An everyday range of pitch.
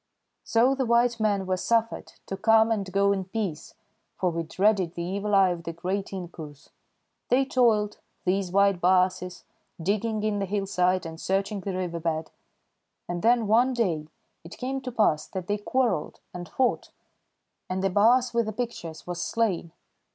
Yes: average, 4.0 semitones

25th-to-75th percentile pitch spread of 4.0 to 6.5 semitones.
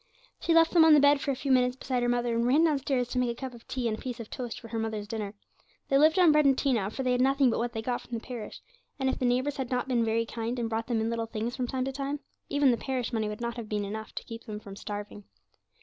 No: average, 2.8 semitones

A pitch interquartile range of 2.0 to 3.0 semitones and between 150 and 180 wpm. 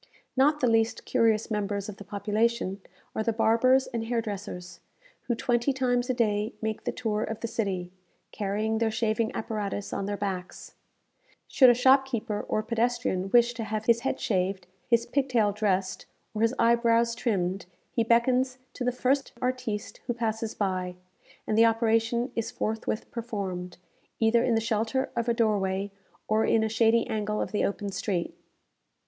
Yes: narrow, 2.4 semitones; average, 170 wpm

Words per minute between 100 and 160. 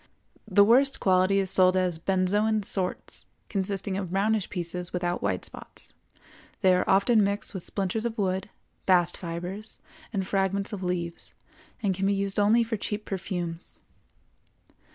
Yes: average, 150 wpm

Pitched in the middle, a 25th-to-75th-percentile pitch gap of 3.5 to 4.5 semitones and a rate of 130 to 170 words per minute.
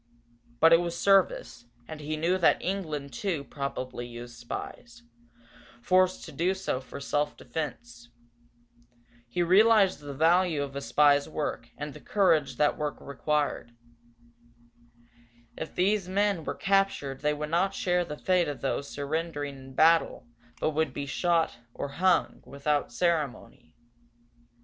Yes: medium, 150 Hz; average, 4.1 semitones; average, 140 wpm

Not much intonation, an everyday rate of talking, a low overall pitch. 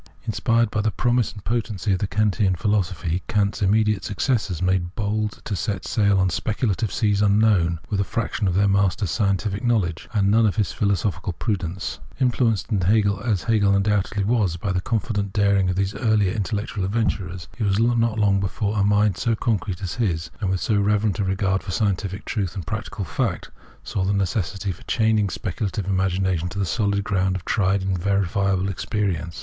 Yes: narrow, 2.3 semitones; average, 180 wpm; low, 100 Hz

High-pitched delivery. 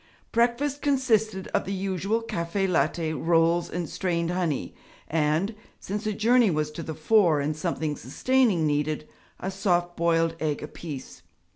No: medium, 175 Hz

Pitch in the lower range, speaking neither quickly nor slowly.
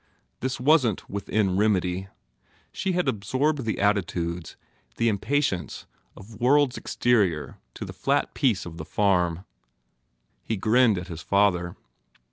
No: low, 100 Hz; slow, 130 wpm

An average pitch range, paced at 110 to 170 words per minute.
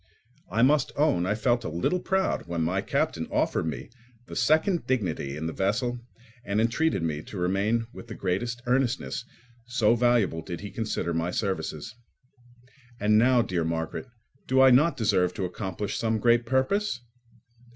No: wide, 5.7 semitones; average, 160 wpm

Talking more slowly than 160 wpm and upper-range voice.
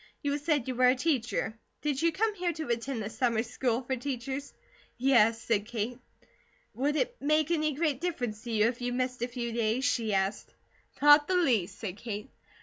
No: average, 195 wpm; very high, 250 Hz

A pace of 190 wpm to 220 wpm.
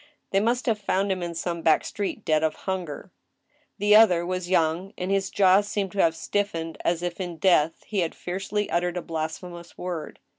Yes: average, 195 wpm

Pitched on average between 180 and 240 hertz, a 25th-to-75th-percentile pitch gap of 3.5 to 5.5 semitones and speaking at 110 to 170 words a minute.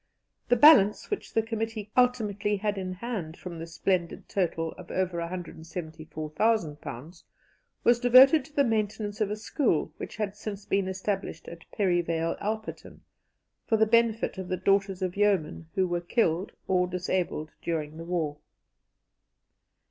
Yes: high, 190 Hz; average, 4.3 semitones; average, 145 wpm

